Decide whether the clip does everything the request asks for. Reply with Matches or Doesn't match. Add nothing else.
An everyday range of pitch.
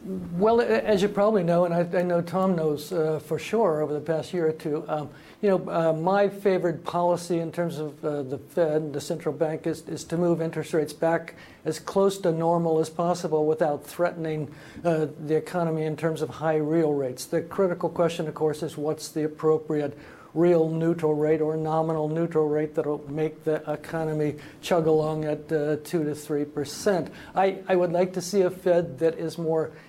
Doesn't match